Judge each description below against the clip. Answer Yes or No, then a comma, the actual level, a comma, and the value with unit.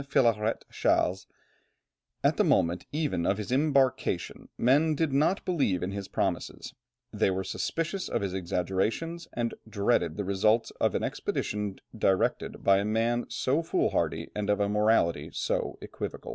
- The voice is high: No, low, 105 Hz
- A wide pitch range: Yes, wide, 6.0 semitones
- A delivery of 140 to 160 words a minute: Yes, average, 155 wpm